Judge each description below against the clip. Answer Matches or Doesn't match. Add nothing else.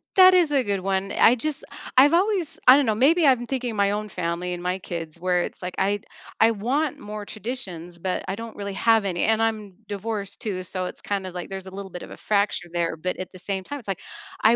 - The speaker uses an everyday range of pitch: Matches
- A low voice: Doesn't match